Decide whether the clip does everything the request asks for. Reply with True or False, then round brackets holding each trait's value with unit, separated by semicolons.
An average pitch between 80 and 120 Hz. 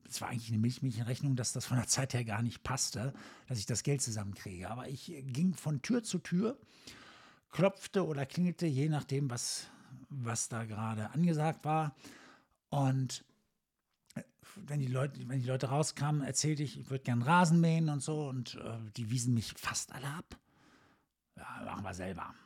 False (135 Hz)